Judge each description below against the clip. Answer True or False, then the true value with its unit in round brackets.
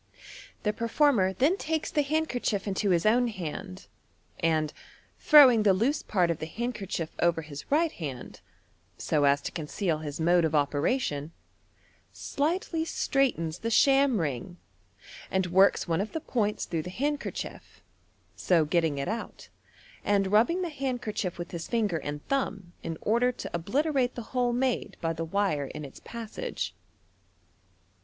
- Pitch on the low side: False (200 Hz)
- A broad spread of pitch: True (7.4 semitones)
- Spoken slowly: False (155 wpm)